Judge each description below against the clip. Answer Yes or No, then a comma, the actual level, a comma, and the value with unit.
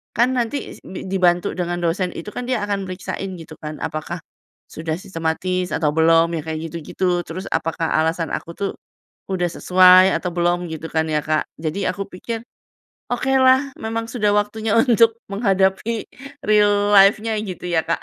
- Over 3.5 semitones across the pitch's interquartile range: Yes, average, 4.0 semitones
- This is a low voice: No, medium, 185 Hz